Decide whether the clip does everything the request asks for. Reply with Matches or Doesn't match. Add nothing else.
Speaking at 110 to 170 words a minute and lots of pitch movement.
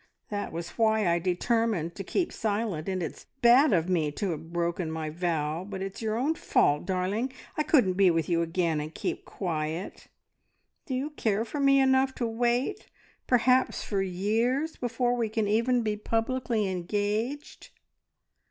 Matches